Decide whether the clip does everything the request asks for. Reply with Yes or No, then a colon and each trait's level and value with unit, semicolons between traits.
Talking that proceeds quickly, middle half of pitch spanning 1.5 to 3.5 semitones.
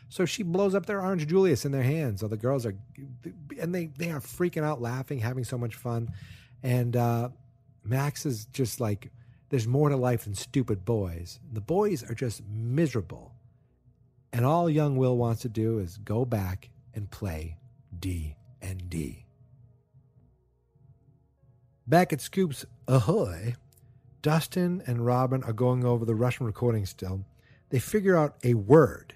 No: average, 160 wpm; average, 3.0 semitones